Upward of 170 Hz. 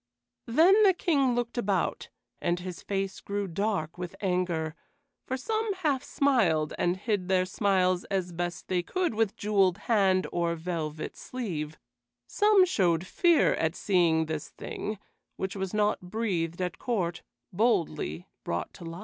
Yes: high, 190 Hz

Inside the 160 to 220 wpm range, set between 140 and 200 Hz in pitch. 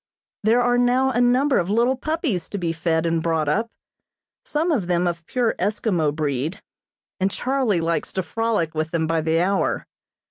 Yes: average, 180 wpm; high, 190 Hz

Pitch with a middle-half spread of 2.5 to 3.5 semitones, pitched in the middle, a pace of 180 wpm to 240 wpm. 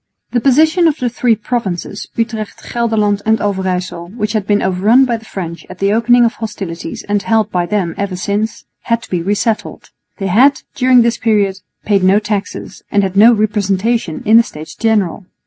No: average, 3.1 semitones; high, 210 Hz; average, 190 wpm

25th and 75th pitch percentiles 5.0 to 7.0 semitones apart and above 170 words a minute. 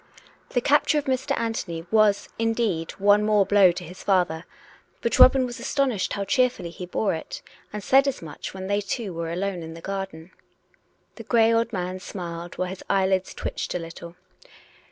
No: average, 4.4 semitones; average, 180 wpm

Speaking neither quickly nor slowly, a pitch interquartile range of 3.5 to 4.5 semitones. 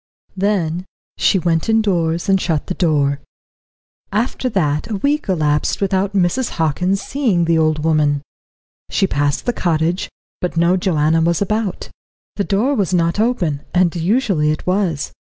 Yes: average, 150 wpm; average, 3.9 semitones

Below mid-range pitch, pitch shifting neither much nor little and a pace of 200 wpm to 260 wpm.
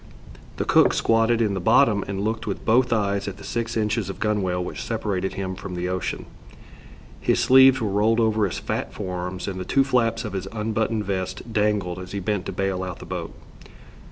Yes: low, 105 Hz; average, 3.1 semitones; fast, 205 wpm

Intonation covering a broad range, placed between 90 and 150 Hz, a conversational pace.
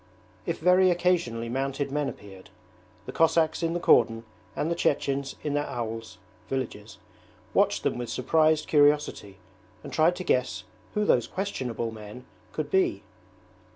Yes: wide, 5.9 semitones; medium, 140 Hz; average, 145 wpm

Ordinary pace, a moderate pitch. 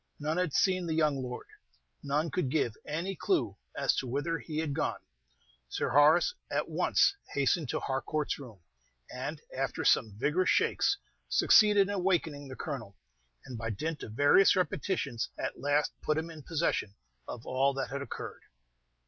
Yes: average, 165 wpm; medium, 150 Hz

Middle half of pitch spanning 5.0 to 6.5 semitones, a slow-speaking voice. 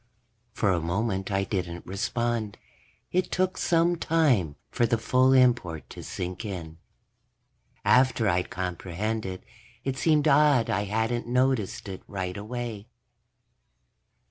Yes: average, 5.3 semitones; slow, 120 wpm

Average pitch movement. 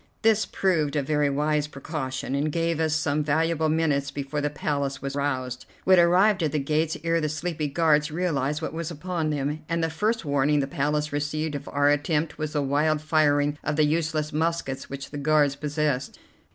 No: narrow, 1.9 semitones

